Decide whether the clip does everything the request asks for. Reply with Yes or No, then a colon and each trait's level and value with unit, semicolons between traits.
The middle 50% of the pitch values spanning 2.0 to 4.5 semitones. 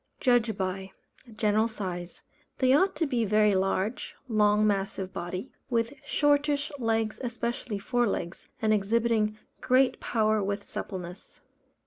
Yes: average, 3.5 semitones